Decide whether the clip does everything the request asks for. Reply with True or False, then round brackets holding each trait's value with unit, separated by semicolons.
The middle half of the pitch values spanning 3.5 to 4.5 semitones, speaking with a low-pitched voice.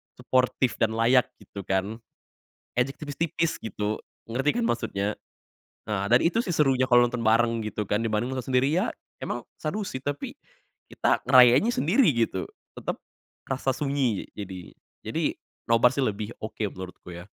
True (4.2 semitones; 120 Hz)